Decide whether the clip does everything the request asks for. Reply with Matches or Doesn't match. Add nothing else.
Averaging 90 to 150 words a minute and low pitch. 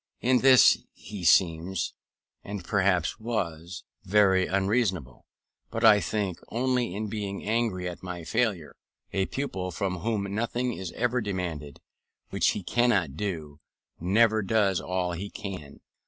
Matches